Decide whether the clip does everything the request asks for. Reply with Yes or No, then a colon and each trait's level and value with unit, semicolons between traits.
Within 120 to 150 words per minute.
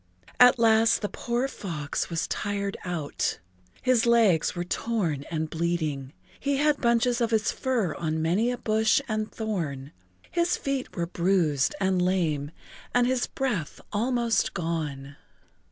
Yes: average, 145 wpm